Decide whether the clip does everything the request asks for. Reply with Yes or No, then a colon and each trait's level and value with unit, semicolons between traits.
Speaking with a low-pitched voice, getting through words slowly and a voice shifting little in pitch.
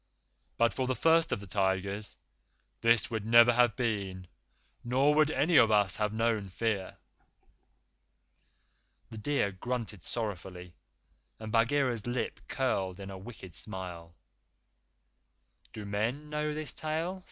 No: low, 110 Hz; slow, 130 wpm; average, 4.6 semitones